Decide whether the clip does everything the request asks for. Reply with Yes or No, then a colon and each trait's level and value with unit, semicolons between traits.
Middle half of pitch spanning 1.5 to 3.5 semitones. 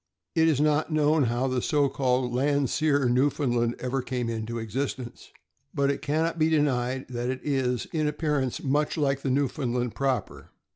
Yes: average, 2.9 semitones